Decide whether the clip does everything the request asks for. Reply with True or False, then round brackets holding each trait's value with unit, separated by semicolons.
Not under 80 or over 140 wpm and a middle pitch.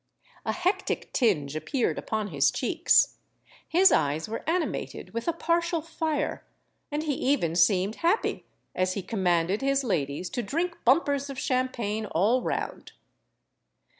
False (135 wpm; 245 Hz)